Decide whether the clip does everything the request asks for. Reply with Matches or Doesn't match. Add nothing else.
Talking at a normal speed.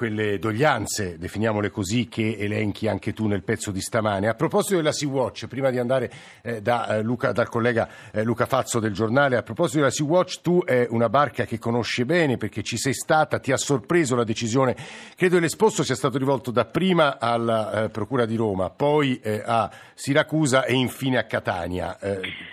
Doesn't match